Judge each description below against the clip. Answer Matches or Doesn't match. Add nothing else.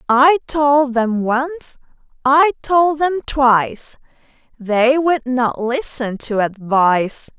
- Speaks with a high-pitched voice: Matches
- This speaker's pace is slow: Matches